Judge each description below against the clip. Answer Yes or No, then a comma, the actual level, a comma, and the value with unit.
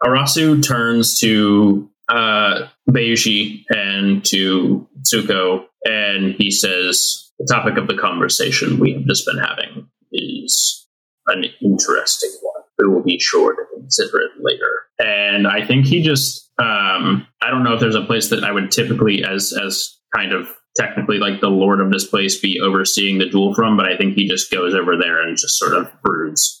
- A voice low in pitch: Yes, low, 105 Hz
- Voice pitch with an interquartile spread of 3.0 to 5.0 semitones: No, wide, 5.4 semitones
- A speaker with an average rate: Yes, average, 175 wpm